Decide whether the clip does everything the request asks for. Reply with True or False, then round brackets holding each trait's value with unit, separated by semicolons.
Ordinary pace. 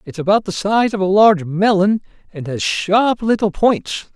True (190 wpm)